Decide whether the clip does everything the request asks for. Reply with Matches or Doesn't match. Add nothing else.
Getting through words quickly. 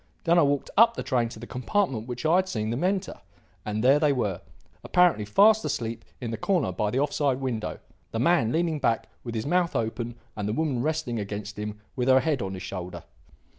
Matches